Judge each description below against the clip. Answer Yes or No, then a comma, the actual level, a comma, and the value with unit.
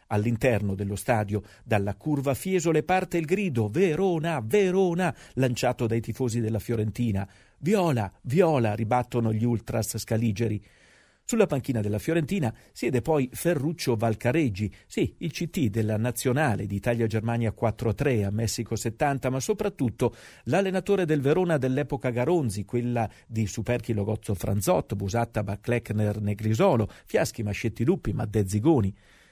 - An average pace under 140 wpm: Yes, average, 120 wpm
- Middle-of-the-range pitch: No, low, 120 Hz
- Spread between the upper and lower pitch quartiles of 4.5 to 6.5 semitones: Yes, average, 4.9 semitones